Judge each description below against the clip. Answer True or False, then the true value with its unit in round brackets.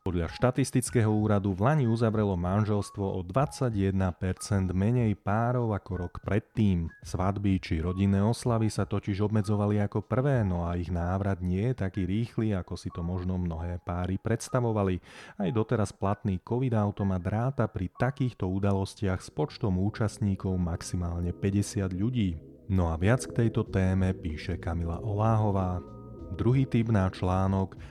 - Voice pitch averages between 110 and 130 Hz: False (100 Hz)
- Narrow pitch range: False (3.2 semitones)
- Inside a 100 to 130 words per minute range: False (140 wpm)